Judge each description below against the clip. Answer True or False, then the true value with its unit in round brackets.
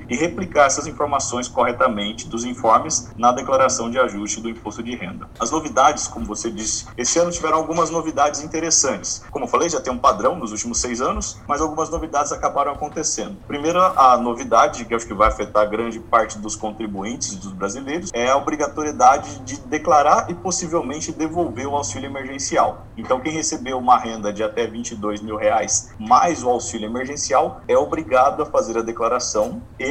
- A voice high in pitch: False (125 Hz)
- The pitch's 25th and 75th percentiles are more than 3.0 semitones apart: True (5.2 semitones)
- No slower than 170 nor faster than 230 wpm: True (180 wpm)